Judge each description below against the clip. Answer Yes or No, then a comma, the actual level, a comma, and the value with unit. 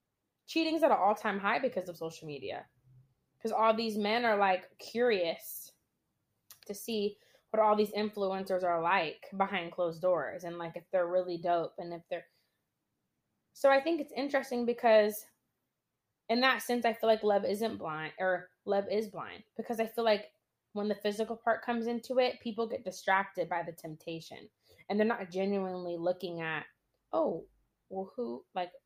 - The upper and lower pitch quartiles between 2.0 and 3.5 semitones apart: No, average, 4.2 semitones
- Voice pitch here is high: Yes, high, 200 Hz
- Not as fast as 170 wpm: No, average, 175 wpm